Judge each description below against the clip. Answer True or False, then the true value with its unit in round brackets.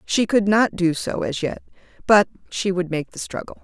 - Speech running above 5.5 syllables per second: False (5.0 syllables/s)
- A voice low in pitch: False (190 Hz)